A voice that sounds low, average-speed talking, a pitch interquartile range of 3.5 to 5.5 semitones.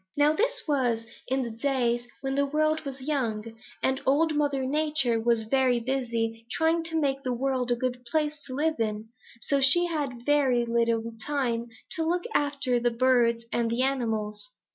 No: very high, 260 Hz; average, 175 wpm; average, 3.8 semitones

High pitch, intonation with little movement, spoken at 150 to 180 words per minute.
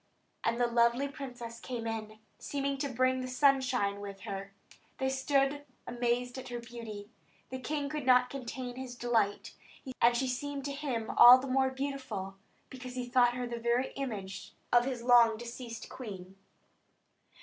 Yes: high, 245 Hz; narrow, 2.2 semitones; average, 165 wpm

